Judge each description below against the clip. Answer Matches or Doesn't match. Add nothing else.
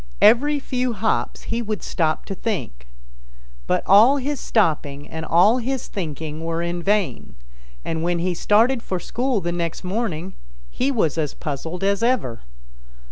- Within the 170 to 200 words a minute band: Doesn't match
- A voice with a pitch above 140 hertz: Matches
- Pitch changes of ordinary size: Doesn't match